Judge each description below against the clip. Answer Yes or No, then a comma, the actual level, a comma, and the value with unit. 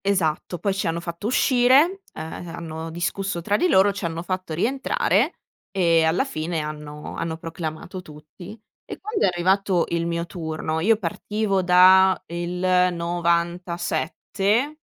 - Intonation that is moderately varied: Yes, average, 3.0 semitones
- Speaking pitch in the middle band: Yes, medium, 175 Hz